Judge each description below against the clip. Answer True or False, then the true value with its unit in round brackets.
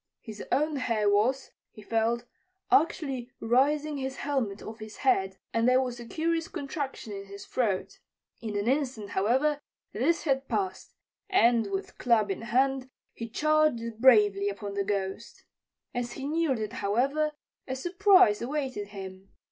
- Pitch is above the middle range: True (240 Hz)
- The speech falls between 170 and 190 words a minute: False (150 wpm)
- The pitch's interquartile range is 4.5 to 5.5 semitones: True (4.9 semitones)